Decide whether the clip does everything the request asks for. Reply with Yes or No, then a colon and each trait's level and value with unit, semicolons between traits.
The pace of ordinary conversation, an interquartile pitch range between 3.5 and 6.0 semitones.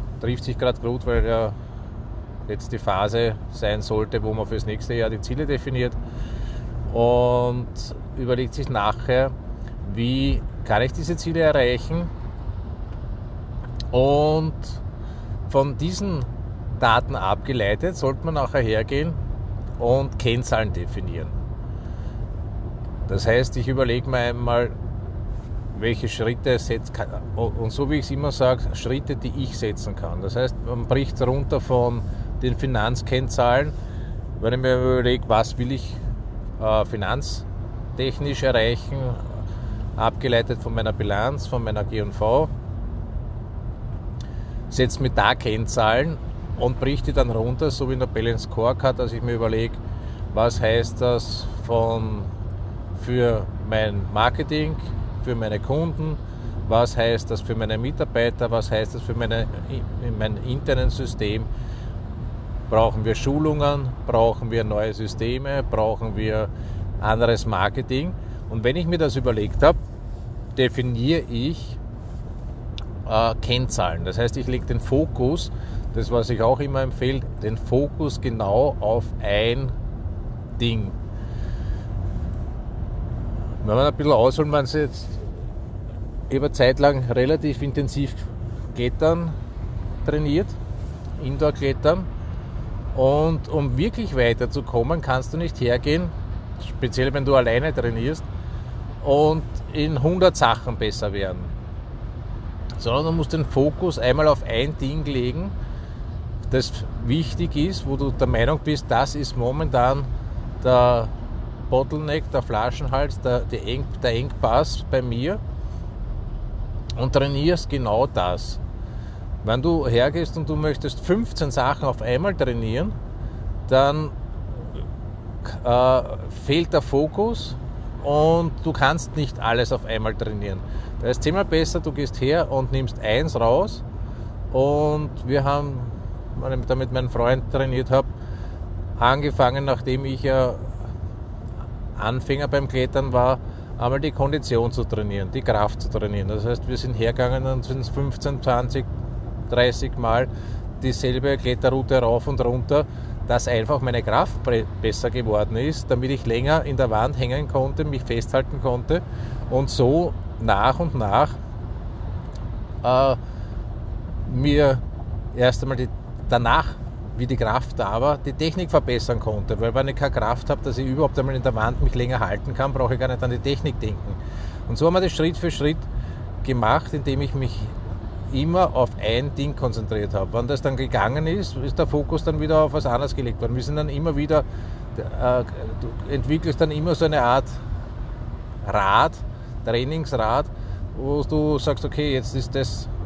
Yes: average, 135 wpm; average, 3.9 semitones